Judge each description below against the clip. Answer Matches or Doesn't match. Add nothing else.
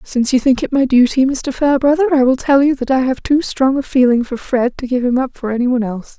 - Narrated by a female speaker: Matches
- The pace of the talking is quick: Matches